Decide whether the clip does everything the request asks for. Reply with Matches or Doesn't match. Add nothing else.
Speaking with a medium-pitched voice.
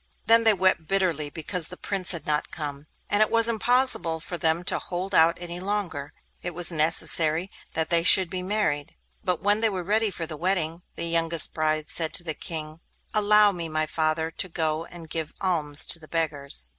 Matches